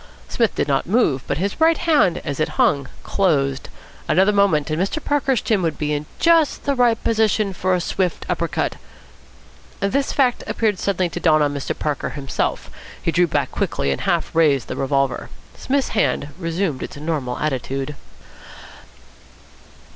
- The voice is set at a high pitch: No, medium, 175 Hz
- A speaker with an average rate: Yes, average, 165 wpm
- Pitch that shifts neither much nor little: No, wide, 6.9 semitones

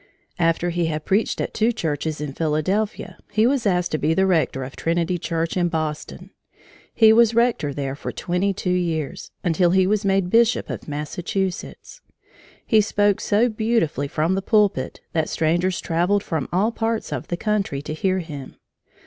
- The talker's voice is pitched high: No, medium, 180 Hz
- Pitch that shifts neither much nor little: Yes, average, 4.5 semitones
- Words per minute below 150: No, average, 175 wpm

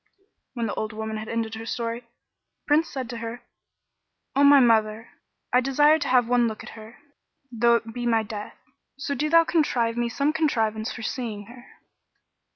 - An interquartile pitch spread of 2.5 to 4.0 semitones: Yes, average, 3.4 semitones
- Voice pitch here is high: Yes, high, 235 Hz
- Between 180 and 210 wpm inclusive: Yes, average, 190 wpm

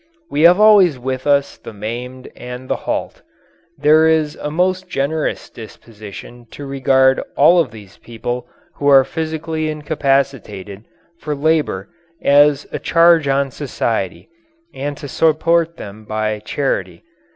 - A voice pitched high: No, medium, 140 Hz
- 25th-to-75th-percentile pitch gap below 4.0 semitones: No, average, 4.7 semitones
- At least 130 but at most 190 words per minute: Yes, slow, 135 wpm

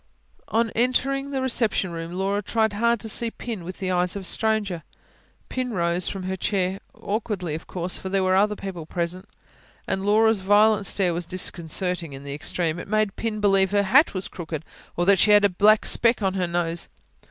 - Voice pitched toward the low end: No, high, 195 Hz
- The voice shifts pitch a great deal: No, average, 3.3 semitones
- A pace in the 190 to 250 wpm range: Yes, average, 200 wpm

